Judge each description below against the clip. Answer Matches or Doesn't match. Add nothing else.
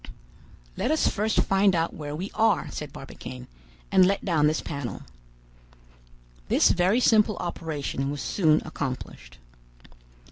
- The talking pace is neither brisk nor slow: Doesn't match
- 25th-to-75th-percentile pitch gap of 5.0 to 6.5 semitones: Matches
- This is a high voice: Doesn't match